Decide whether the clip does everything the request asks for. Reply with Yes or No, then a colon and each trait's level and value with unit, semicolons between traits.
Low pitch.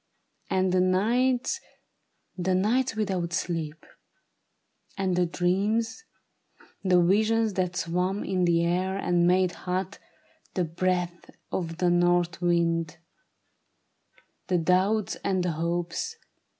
No: medium, 180 Hz